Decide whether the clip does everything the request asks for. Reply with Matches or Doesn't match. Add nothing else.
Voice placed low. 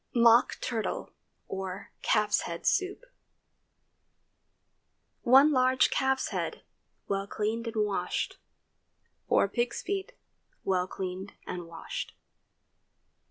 Doesn't match